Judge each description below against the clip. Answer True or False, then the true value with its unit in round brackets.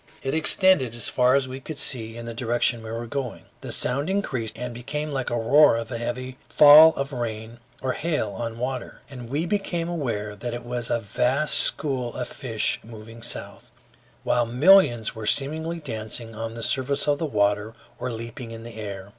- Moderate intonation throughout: True (3.6 semitones)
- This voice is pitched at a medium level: False (120 Hz)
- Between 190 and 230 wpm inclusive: True (195 wpm)